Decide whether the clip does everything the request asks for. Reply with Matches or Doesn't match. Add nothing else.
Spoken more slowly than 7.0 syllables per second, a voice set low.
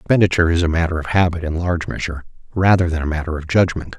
Doesn't match